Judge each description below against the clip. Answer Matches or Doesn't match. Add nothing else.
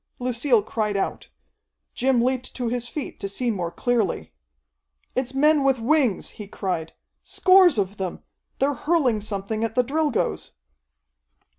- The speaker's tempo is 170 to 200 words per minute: Doesn't match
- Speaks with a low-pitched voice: Doesn't match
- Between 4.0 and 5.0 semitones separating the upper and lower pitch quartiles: Matches